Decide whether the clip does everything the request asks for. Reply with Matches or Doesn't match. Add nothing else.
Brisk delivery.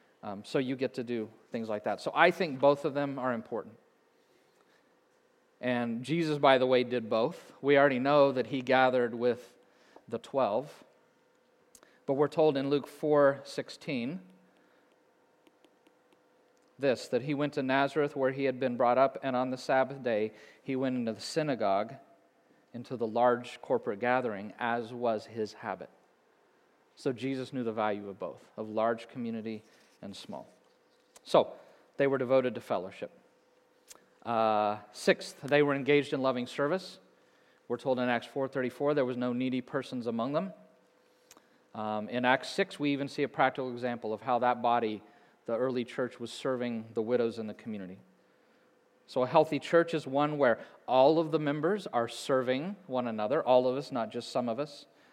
Doesn't match